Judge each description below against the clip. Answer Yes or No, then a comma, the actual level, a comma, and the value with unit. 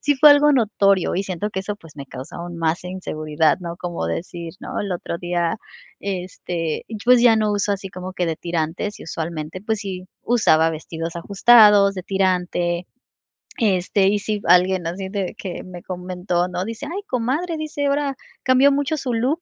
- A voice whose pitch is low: No, medium, 185 Hz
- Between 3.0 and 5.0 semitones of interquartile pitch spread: Yes, average, 4.3 semitones